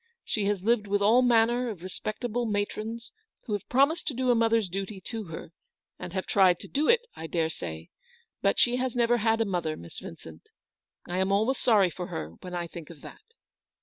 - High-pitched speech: Yes, high, 210 Hz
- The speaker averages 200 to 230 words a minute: Yes, fast, 205 wpm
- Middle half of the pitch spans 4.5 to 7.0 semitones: Yes, average, 5.0 semitones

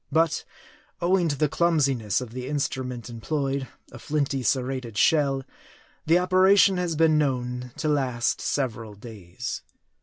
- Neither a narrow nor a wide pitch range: Yes, average, 4.1 semitones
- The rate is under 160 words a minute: Yes, average, 140 wpm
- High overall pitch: No, low, 135 Hz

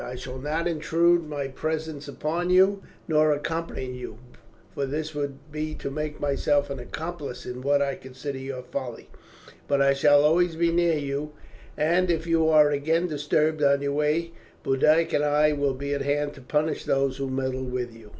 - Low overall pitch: No, medium, 145 Hz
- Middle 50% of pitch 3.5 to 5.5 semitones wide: No, narrow, 2.4 semitones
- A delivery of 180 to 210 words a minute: Yes, average, 185 wpm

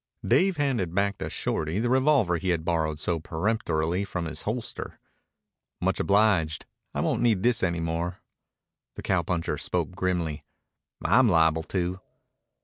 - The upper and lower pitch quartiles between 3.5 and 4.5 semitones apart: No, average, 4.9 semitones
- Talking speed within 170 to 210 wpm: No, average, 140 wpm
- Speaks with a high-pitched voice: No, very low, 90 Hz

